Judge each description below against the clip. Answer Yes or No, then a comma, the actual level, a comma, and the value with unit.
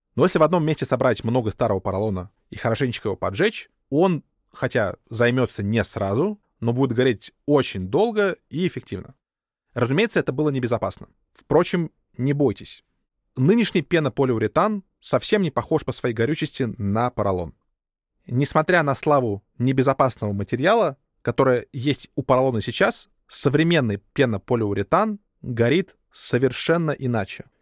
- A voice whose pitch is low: Yes, low, 130 Hz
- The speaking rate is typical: Yes, average, 125 wpm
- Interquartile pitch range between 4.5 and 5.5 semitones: Yes, average, 5.2 semitones